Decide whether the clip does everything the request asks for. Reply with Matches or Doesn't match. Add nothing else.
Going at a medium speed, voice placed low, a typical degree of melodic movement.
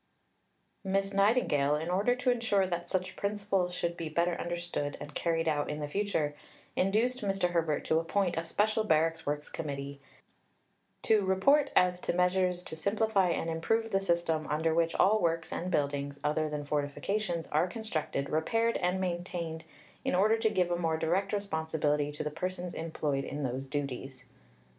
Doesn't match